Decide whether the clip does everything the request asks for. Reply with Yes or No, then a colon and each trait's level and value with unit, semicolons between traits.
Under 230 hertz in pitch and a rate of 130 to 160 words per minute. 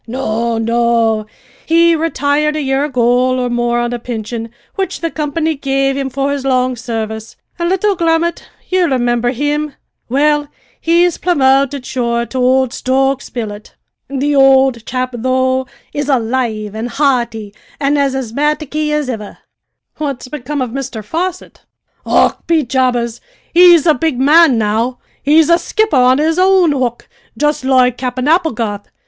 No: very high, 265 Hz; average, 150 wpm